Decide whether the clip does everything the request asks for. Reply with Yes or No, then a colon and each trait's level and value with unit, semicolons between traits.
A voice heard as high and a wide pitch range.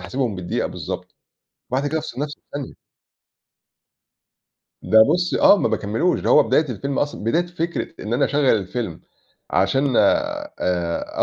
No: medium, 140 Hz; wide, 7.4 semitones